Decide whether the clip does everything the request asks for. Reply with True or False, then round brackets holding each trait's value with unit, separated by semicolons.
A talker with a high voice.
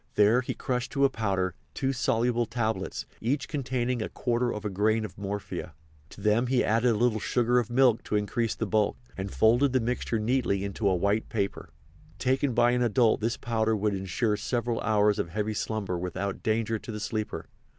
False (110 Hz)